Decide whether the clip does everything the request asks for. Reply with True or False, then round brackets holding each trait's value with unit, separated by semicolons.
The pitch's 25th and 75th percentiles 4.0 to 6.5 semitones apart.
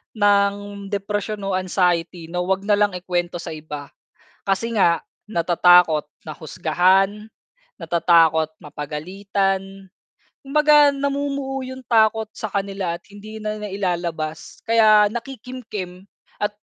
False (3.5 semitones)